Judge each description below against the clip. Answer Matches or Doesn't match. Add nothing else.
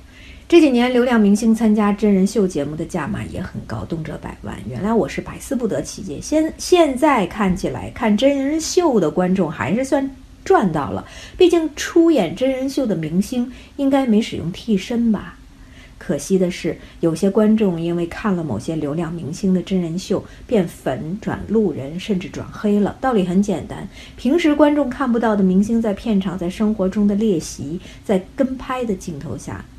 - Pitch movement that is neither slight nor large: Doesn't match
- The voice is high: Matches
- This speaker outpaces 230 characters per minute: Matches